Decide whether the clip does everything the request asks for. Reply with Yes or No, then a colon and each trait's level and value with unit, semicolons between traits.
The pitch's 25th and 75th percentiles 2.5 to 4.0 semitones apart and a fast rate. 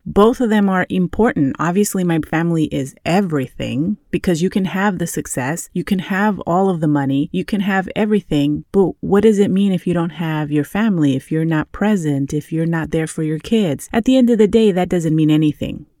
No: average, 4.6 semitones; fast, 220 wpm